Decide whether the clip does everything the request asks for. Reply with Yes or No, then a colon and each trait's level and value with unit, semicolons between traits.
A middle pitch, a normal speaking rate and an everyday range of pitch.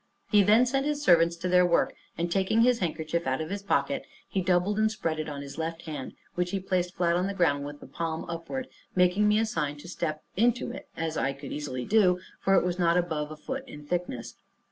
No: medium, 175 Hz; fast, 235 wpm; average, 4.2 semitones